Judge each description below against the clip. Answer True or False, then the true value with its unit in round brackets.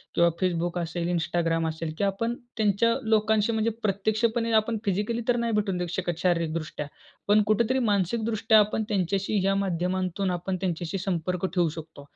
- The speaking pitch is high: True (195 Hz)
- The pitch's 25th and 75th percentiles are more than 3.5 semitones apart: True (3.9 semitones)